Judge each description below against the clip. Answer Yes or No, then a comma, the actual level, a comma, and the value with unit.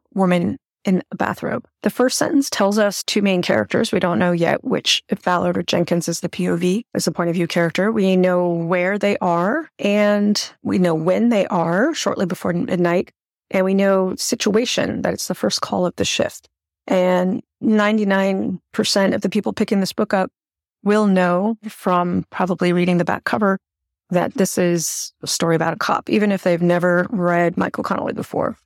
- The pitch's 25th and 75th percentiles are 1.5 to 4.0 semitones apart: Yes, average, 2.8 semitones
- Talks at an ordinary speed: Yes, average, 190 wpm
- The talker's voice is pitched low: No, high, 190 Hz